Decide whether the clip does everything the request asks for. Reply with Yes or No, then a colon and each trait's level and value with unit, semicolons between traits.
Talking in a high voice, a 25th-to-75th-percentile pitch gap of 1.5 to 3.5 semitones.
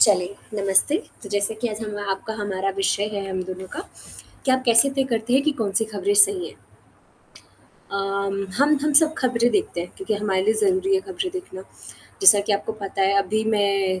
No: high, 210 Hz; wide, 5.4 semitones